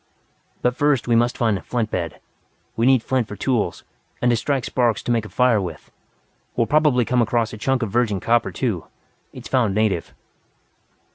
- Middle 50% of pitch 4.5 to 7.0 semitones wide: No, average, 2.7 semitones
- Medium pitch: No, low, 120 Hz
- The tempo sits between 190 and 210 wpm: Yes, average, 195 wpm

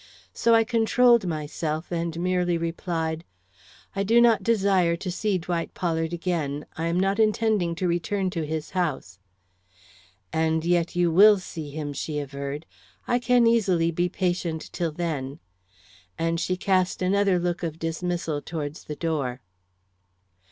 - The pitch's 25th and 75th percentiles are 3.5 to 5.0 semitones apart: No, average, 2.9 semitones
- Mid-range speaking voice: Yes, medium, 170 Hz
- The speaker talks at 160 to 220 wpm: No, average, 145 wpm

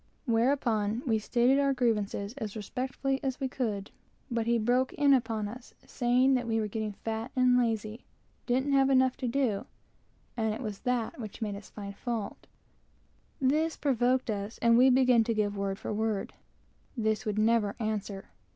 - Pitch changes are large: No, average, 3.1 semitones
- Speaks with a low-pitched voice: No, high, 230 Hz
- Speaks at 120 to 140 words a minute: No, average, 160 wpm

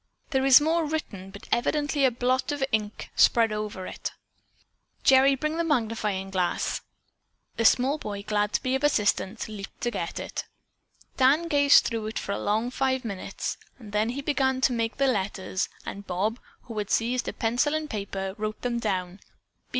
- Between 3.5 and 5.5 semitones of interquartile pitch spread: Yes, average, 4.5 semitones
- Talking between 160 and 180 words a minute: Yes, average, 175 wpm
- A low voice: No, high, 230 Hz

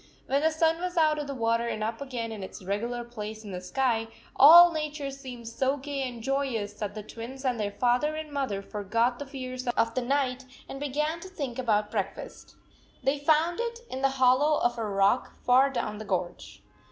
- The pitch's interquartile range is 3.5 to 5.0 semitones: Yes, average, 4.2 semitones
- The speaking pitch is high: Yes, very high, 255 Hz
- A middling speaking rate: No, fast, 210 wpm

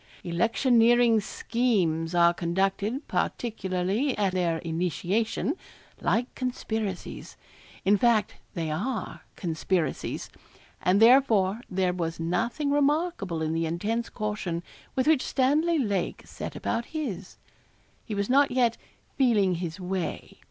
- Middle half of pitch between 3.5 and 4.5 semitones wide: No, wide, 5.4 semitones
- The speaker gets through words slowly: Yes, slow, 115 wpm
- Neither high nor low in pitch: No, high, 205 Hz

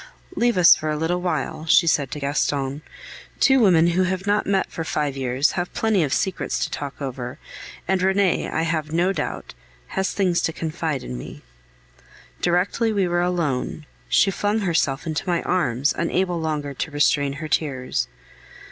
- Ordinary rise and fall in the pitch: Yes, average, 4.2 semitones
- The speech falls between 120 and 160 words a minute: No, average, 170 wpm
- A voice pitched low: No, medium, 165 Hz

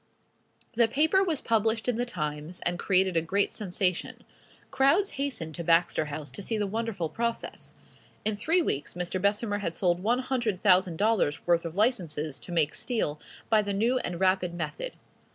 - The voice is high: Yes, high, 195 Hz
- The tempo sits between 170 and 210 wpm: Yes, average, 175 wpm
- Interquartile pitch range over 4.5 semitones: Yes, average, 5.2 semitones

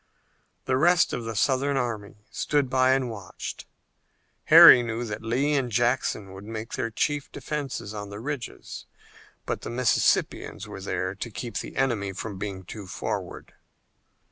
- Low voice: Yes, low, 115 Hz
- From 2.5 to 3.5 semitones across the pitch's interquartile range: No, average, 4.2 semitones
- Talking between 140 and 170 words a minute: Yes, average, 155 wpm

